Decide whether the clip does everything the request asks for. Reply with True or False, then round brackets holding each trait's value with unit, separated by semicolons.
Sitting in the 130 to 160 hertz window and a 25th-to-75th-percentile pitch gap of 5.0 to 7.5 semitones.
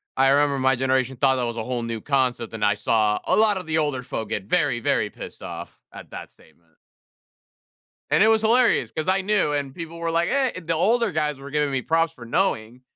True (140 Hz; 5.4 semitones)